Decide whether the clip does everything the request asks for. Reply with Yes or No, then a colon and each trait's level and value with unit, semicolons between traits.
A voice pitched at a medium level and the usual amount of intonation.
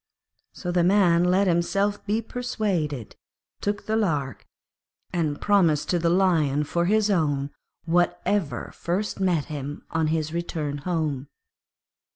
Yes: medium, 170 Hz; average, 4.5 semitones